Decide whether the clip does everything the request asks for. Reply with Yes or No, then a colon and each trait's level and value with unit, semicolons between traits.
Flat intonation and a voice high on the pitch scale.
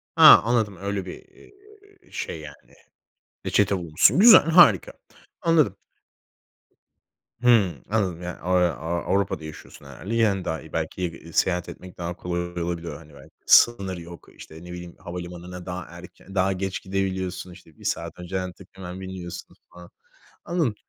No: narrow, 2.2 semitones; very low, 90 Hz